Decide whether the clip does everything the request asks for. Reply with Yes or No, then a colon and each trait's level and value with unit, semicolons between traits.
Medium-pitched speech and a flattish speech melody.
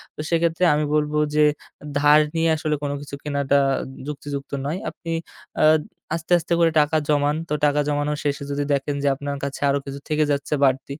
Yes: medium, 145 Hz; narrow, 1.3 semitones